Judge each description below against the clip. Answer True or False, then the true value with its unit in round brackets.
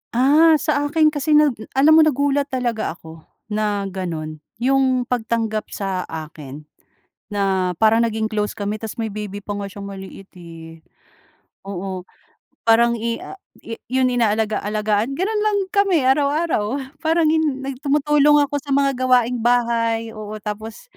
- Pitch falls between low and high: False (230 Hz)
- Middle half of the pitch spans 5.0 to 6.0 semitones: True (5.5 semitones)